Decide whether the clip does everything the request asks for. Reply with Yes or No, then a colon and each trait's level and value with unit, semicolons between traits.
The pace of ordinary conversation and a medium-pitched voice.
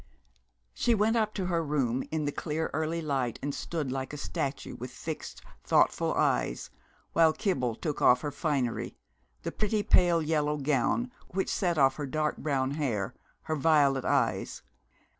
Yes: average, 160 wpm; medium, 150 Hz